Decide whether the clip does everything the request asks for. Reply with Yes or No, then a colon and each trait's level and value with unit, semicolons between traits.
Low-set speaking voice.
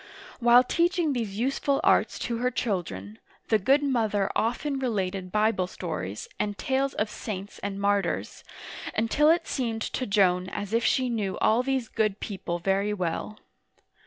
No: high, 215 Hz